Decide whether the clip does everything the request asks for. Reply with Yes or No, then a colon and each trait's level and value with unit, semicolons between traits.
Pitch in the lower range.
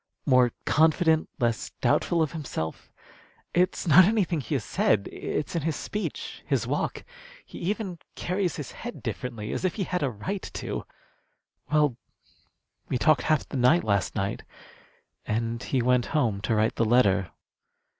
No: medium, 145 Hz